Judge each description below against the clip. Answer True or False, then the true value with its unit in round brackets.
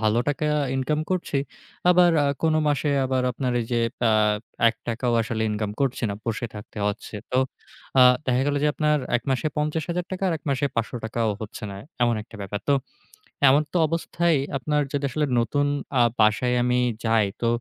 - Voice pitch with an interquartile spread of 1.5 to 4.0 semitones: False (4.7 semitones)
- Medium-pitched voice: False (130 Hz)